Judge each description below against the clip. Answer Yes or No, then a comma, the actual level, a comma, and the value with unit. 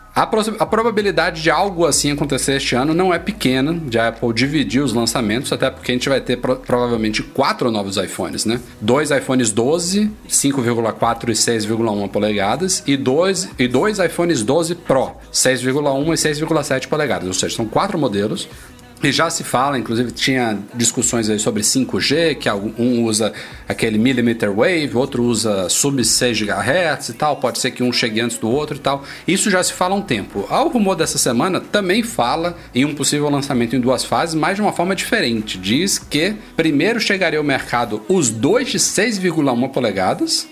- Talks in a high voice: No, low, 135 Hz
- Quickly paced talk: No, average, 175 wpm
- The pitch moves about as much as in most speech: No, wide, 6.0 semitones